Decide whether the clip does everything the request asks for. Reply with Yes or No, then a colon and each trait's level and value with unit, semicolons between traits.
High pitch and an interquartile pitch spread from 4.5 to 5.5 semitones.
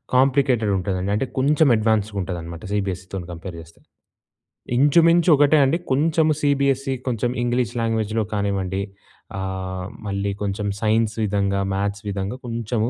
No: low, 105 Hz; average, 5.1 semitones